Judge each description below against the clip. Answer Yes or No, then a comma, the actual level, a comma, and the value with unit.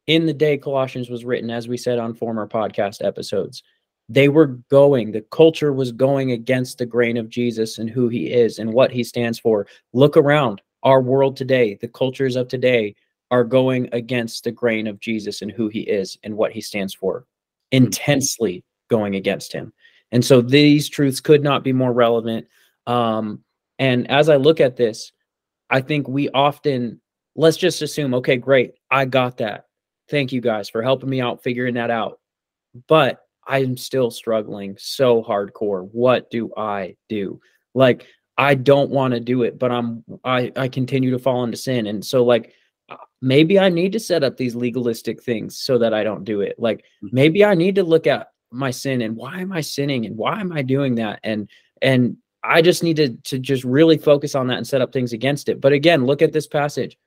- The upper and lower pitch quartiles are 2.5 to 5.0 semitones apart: Yes, average, 3.0 semitones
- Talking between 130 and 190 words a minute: No, average, 200 wpm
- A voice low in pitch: Yes, low, 125 Hz